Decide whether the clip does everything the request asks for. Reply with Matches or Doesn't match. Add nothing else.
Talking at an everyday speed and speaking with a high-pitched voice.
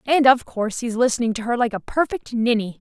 Doesn't match